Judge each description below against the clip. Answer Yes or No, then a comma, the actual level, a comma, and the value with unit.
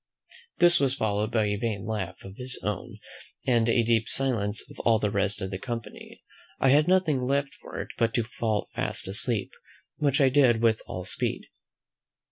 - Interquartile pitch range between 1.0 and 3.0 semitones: No, average, 4.1 semitones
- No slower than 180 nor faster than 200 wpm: Yes, average, 185 wpm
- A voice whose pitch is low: Yes, low, 115 Hz